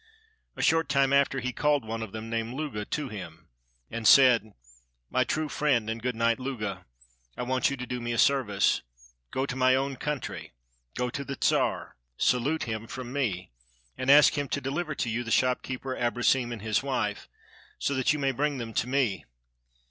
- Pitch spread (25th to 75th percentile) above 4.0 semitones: No, average, 3.3 semitones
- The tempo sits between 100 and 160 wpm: No, average, 195 wpm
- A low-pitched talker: Yes, low, 125 Hz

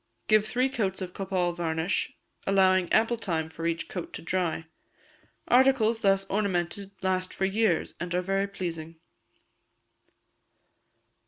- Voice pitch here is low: No, high, 190 Hz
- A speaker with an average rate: No, slow, 130 wpm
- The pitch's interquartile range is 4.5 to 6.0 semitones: No, average, 2.7 semitones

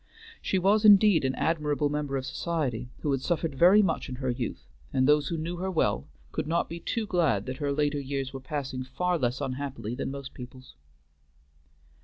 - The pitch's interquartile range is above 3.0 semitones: Yes, average, 4.4 semitones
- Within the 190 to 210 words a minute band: Yes, average, 195 wpm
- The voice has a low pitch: No, medium, 145 Hz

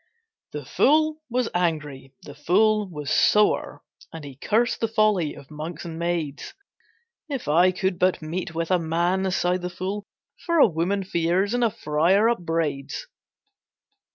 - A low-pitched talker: No, medium, 180 Hz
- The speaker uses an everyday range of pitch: Yes, average, 4.4 semitones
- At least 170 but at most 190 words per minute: No, average, 155 wpm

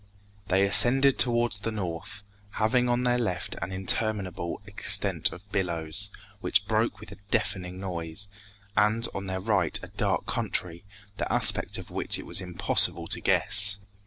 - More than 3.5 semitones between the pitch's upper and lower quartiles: No, average, 3.0 semitones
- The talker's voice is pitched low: Yes, low, 100 Hz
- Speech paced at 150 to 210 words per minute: Yes, average, 155 wpm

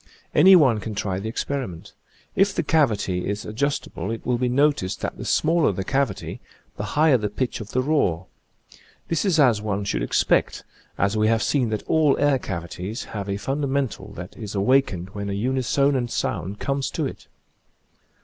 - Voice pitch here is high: No, low, 115 Hz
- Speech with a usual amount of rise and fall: No, wide, 5.9 semitones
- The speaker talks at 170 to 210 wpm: Yes, average, 180 wpm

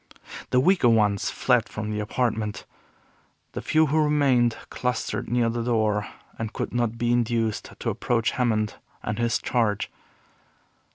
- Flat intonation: Yes, narrow, 2.3 semitones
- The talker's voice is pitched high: No, low, 115 Hz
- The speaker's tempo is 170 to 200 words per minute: No, average, 145 wpm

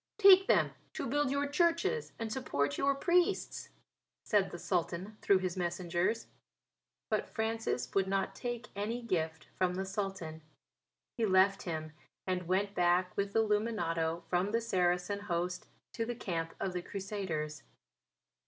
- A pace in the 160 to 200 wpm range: No, average, 145 wpm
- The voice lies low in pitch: No, high, 195 Hz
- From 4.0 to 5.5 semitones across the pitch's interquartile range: Yes, average, 4.4 semitones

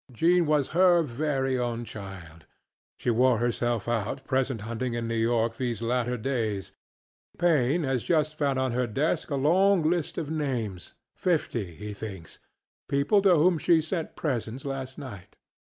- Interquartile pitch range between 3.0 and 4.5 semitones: No, average, 5.0 semitones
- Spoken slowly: No, average, 145 wpm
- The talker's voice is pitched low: Yes, low, 130 Hz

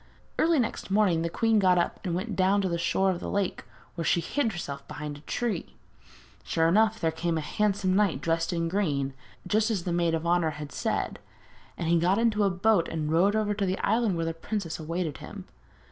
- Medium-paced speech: No, fast, 220 wpm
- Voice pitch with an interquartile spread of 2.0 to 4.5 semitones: Yes, average, 3.9 semitones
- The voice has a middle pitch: Yes, medium, 180 Hz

